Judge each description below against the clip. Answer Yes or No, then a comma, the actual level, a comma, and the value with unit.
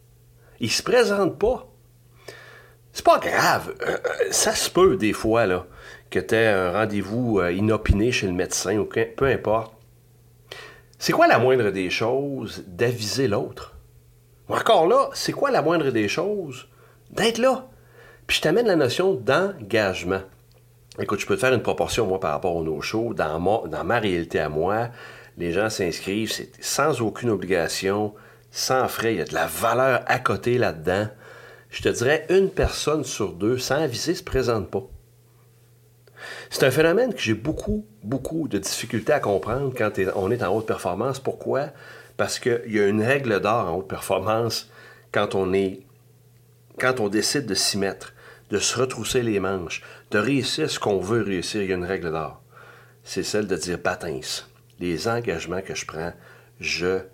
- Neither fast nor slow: Yes, average, 175 wpm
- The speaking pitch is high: No, low, 115 Hz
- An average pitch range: Yes, average, 4.2 semitones